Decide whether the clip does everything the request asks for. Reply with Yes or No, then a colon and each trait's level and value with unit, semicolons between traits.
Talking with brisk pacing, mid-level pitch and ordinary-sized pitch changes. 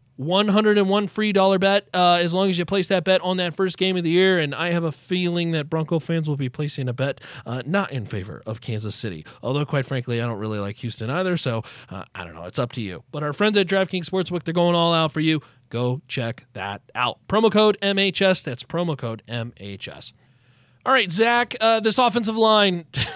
No: fast, 225 wpm; medium, 160 Hz; wide, 7.3 semitones